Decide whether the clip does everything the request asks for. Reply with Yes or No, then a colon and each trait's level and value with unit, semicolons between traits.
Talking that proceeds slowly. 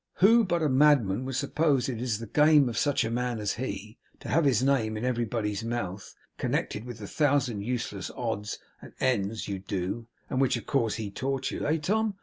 No: fast, 205 wpm